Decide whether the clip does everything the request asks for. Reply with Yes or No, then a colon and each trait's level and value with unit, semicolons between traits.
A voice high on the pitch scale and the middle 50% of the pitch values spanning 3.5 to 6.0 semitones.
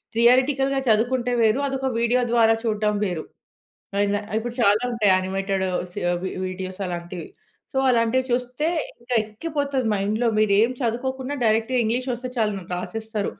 Yes: high, 225 Hz; average, 3.8 semitones